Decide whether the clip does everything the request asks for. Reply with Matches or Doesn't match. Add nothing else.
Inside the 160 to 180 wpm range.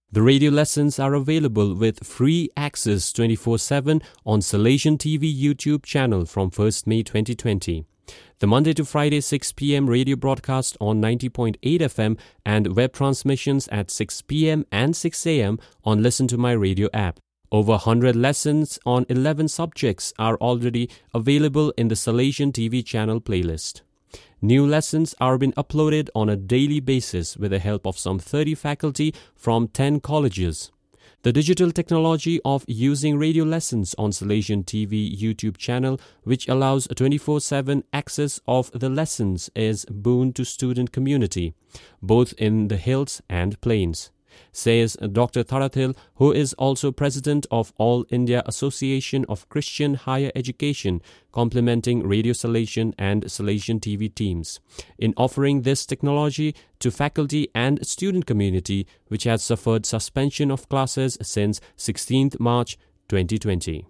Doesn't match